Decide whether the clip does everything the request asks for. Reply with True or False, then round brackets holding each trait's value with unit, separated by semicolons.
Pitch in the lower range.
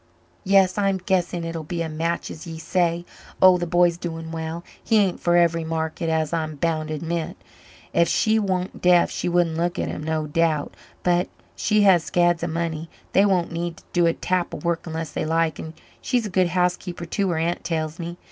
False (170 Hz)